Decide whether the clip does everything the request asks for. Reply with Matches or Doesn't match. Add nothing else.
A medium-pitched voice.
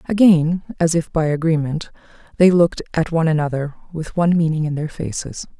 Matches